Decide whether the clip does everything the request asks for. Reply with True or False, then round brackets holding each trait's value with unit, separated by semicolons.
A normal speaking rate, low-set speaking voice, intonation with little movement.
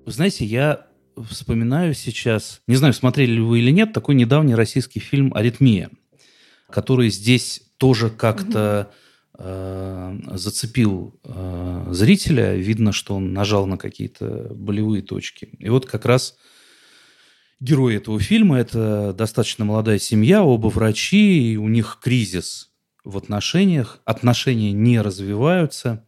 False (125 wpm; 115 Hz; 3.9 semitones)